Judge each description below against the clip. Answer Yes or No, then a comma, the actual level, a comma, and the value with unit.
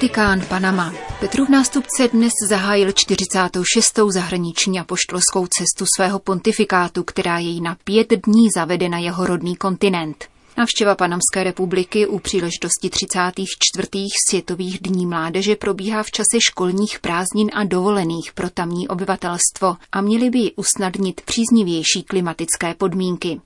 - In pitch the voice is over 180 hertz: Yes, high, 190 Hz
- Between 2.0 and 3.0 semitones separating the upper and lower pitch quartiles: Yes, narrow, 2.6 semitones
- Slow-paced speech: No, average, 125 wpm